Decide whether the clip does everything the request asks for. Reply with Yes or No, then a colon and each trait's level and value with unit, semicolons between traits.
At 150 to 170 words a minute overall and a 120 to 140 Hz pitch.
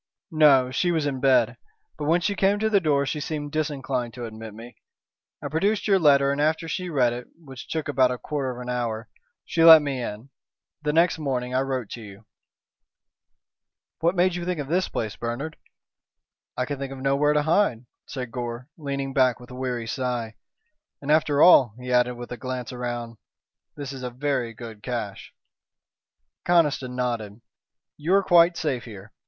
No: average, 185 wpm; low, 135 Hz